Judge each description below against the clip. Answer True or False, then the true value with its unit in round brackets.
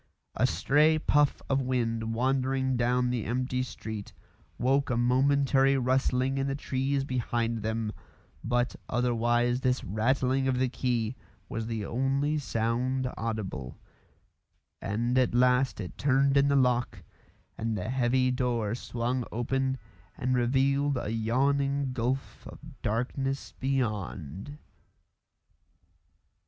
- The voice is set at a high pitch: False (125 Hz)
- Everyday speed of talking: False (120 wpm)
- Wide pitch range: False (2.4 semitones)